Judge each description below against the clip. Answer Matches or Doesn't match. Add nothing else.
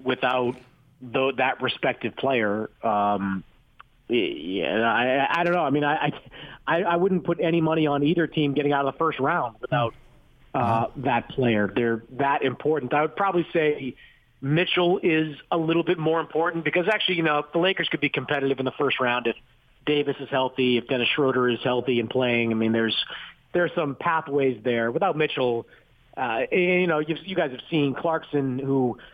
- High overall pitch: Doesn't match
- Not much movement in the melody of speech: Doesn't match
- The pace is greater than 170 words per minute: Matches